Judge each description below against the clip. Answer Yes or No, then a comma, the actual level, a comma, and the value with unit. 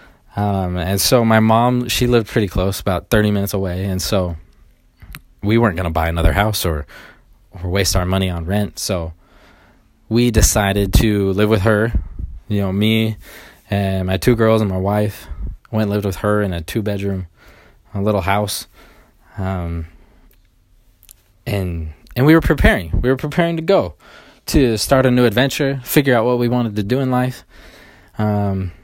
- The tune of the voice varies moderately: Yes, average, 3.4 semitones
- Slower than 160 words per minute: No, average, 175 wpm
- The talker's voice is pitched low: Yes, low, 100 Hz